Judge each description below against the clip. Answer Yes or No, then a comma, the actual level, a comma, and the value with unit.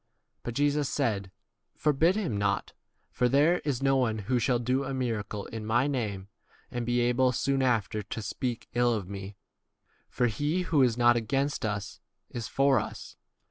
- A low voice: Yes, low, 120 Hz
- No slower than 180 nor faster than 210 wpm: Yes, average, 185 wpm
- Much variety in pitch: No, average, 3.9 semitones